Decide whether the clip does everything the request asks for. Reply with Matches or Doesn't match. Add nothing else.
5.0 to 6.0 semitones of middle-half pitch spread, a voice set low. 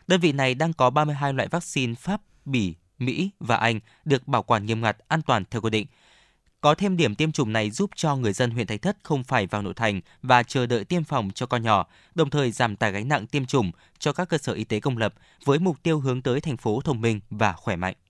Matches